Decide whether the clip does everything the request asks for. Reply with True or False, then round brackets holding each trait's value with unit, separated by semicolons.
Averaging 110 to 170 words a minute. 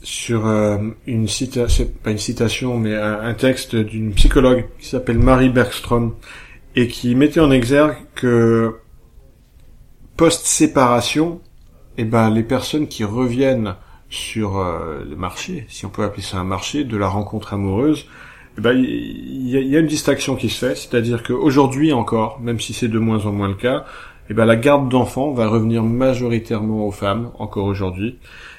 True (160 wpm)